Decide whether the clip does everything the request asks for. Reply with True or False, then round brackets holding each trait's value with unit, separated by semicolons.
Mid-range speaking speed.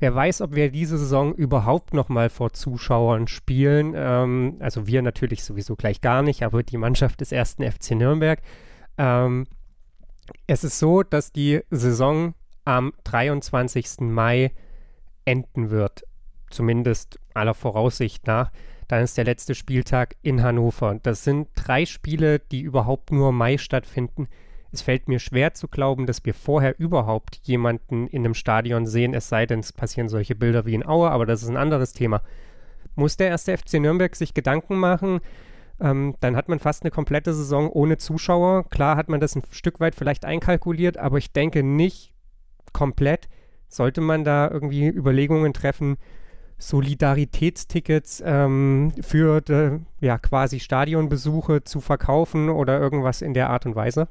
True (155 wpm)